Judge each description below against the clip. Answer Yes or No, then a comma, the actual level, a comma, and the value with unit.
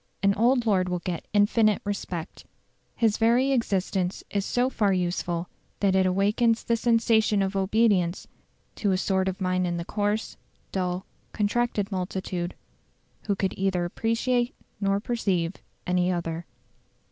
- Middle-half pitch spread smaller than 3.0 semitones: No, average, 3.4 semitones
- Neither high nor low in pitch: No, high, 195 Hz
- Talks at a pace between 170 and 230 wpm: No, average, 140 wpm